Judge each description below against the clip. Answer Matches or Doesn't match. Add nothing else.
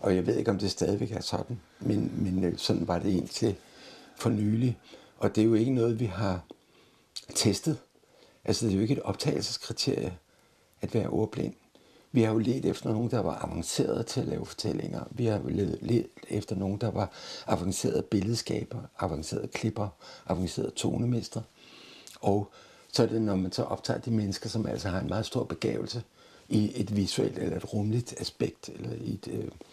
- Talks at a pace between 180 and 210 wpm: Matches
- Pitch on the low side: Matches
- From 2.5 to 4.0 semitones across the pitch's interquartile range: Matches